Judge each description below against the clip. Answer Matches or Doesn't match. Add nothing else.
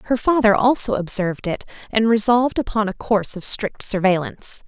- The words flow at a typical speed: Matches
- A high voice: Matches